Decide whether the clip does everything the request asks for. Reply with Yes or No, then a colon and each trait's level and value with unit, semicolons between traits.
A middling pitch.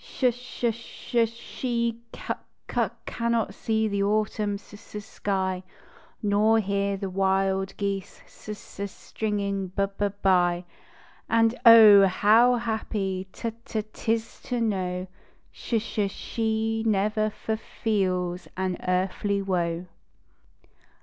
No: high, 205 Hz